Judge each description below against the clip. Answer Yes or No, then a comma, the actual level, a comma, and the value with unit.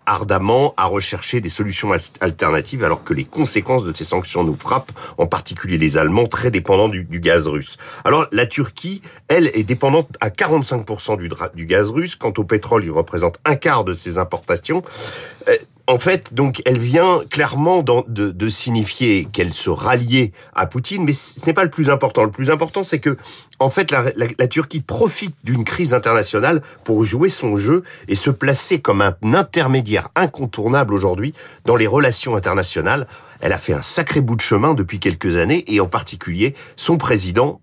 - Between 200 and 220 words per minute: No, average, 185 wpm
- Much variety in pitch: Yes, wide, 6.9 semitones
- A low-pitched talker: Yes, low, 125 Hz